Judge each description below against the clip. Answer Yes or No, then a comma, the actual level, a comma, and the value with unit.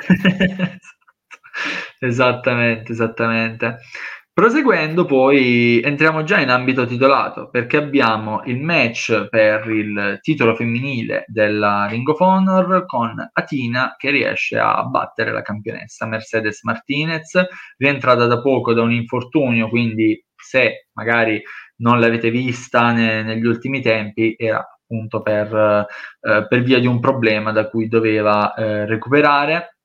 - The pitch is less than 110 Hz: No, low, 120 Hz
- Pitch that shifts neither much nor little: Yes, average, 3.5 semitones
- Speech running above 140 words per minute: No, average, 125 wpm